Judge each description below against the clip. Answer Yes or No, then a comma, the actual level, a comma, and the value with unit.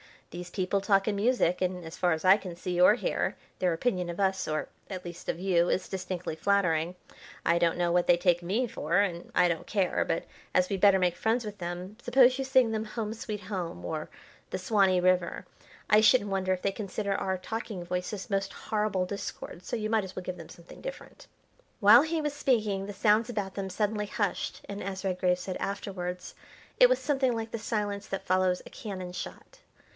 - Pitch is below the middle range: No, high, 195 Hz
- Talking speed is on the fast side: Yes, fast, 210 wpm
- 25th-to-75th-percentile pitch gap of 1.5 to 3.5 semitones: Yes, average, 2.9 semitones